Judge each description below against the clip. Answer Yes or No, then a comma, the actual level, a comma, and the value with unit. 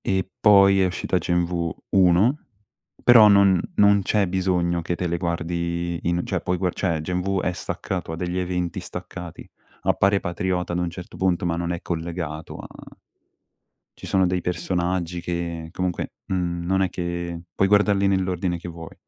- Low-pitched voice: Yes, very low, 90 Hz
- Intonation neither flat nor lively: No, narrow, 1.6 semitones